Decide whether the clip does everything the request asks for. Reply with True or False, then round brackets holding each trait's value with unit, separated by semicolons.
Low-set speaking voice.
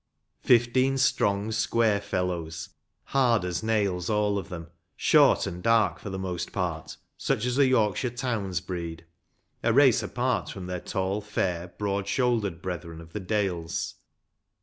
True (100 Hz)